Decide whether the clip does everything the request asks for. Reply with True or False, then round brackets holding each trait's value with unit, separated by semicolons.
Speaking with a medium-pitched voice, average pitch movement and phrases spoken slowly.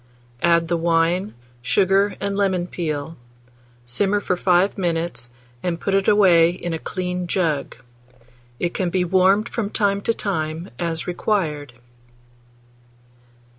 True (180 Hz; 3.0 semitones; 130 wpm)